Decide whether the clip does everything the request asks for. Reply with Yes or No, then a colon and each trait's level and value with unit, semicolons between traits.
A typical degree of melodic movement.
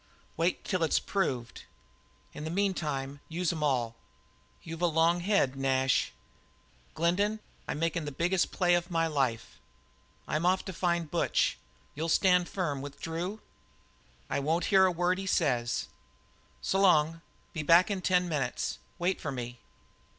Yes: average, 4.0 semitones